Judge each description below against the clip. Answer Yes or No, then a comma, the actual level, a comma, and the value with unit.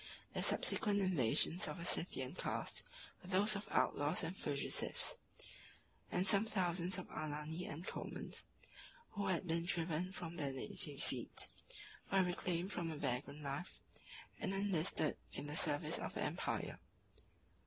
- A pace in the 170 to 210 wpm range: No, average, 145 wpm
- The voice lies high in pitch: No, medium, 175 Hz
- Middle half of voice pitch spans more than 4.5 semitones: No, average, 3.8 semitones